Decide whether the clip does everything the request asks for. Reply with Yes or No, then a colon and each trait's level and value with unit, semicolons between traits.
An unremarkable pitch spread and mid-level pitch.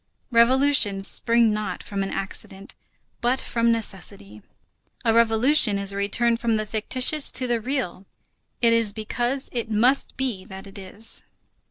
No: average, 3.3 semitones; high, 225 Hz